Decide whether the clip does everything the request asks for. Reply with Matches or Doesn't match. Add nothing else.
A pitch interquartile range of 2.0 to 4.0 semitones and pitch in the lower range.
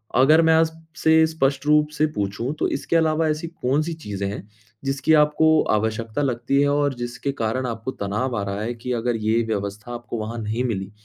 Doesn't match